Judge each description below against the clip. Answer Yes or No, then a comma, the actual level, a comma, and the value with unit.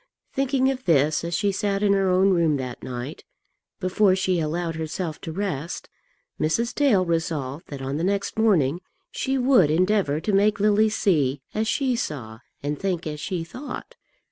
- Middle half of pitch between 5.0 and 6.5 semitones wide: Yes, average, 5.3 semitones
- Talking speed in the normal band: Yes, average, 170 wpm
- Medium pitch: Yes, medium, 180 Hz